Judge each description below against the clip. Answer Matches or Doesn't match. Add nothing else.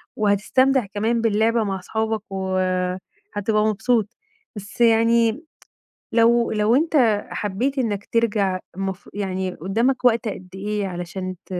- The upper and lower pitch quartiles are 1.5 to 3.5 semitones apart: Matches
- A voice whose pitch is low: Doesn't match